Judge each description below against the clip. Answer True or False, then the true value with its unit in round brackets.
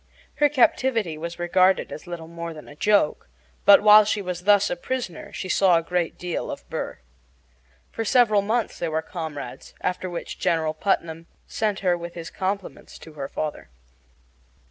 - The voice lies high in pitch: False (180 Hz)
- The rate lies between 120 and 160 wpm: False (170 wpm)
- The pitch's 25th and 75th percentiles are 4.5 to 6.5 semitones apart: False (3.8 semitones)